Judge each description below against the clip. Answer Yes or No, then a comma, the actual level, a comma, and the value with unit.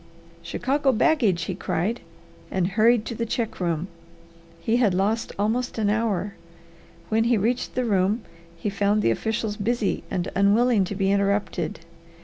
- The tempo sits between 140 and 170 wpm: Yes, average, 150 wpm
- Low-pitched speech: No, high, 210 Hz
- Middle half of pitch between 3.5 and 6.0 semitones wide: No, average, 3.1 semitones